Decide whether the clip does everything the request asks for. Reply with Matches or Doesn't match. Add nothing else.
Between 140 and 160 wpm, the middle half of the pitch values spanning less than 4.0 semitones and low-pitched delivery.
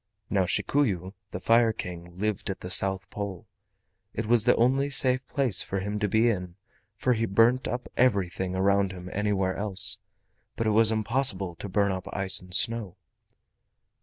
Doesn't match